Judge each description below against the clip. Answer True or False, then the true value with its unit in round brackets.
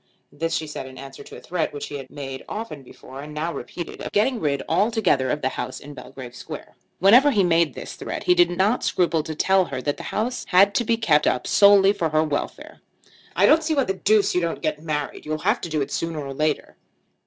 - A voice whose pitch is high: False (165 Hz)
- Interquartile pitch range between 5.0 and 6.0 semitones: True (5.5 semitones)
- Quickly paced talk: True (240 wpm)